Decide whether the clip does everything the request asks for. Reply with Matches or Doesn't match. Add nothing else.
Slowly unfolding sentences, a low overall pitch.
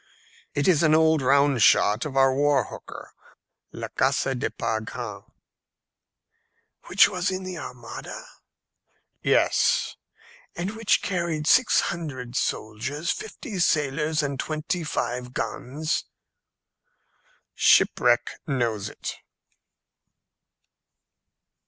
Doesn't match